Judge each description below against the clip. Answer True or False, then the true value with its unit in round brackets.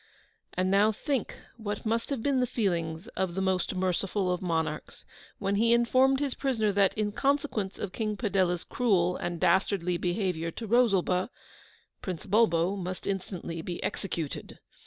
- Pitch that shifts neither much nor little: True (3.8 semitones)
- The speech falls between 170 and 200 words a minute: False (155 wpm)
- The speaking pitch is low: False (195 Hz)